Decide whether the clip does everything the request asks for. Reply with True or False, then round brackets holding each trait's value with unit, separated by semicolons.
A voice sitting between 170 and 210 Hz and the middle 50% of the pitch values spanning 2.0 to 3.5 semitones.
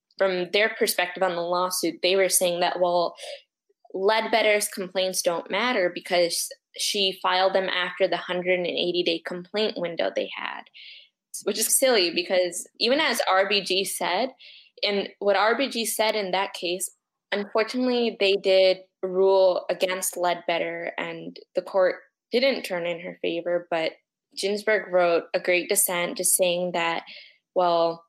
True (185 Hz; 2.5 semitones)